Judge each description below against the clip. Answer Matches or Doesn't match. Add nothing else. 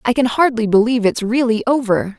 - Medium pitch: Doesn't match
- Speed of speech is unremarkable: Matches